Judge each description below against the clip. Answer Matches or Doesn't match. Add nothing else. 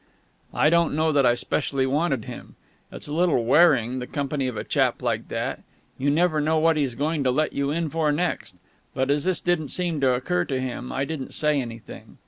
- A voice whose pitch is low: Doesn't match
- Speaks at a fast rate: Matches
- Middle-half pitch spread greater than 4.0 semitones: Doesn't match